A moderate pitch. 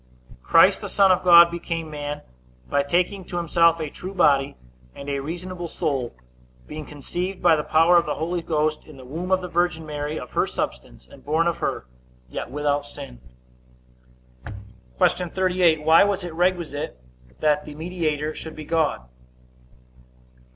Yes: medium, 160 Hz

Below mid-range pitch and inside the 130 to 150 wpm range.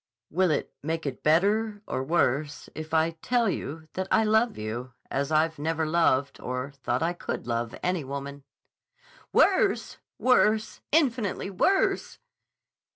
No: medium, 160 Hz; average, 140 wpm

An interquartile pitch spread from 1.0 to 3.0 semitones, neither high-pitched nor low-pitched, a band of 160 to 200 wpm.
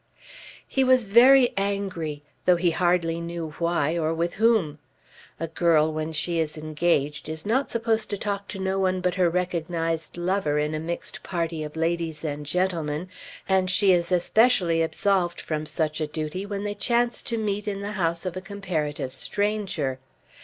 No: average, 3.9 semitones; medium, 175 Hz; average, 175 wpm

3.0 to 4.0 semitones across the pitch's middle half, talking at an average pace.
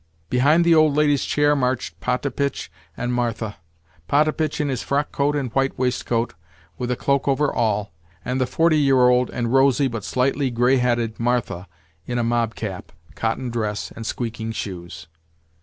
Yes: average, 3.6 semitones; average, 155 wpm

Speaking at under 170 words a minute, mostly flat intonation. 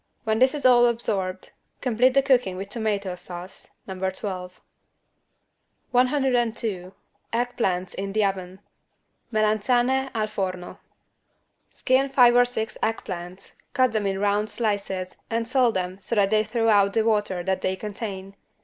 No: average, 150 wpm; average, 4.2 semitones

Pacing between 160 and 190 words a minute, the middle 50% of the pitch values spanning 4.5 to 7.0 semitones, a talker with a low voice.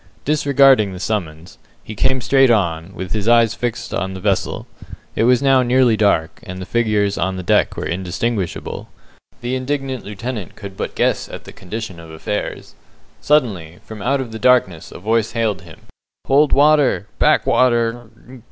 Yes: average, 170 wpm; average, 5.2 semitones; low, 110 Hz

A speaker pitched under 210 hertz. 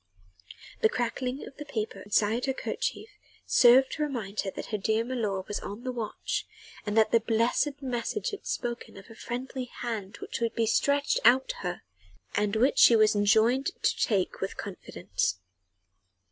No: high, 230 Hz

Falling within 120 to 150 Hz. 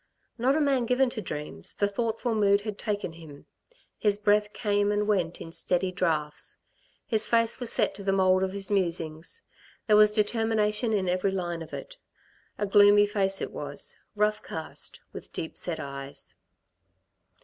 No: high, 205 Hz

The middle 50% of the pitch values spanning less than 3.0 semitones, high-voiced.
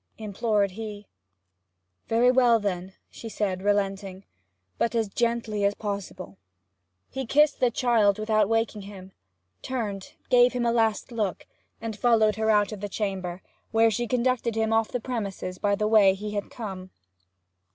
Yes: narrow, 2.6 semitones; high, 215 Hz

